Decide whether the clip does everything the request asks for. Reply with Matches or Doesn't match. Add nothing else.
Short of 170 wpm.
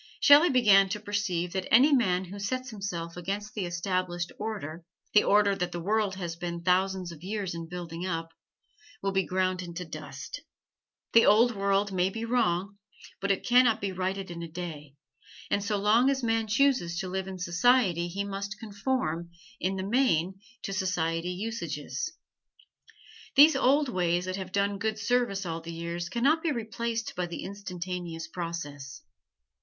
Doesn't match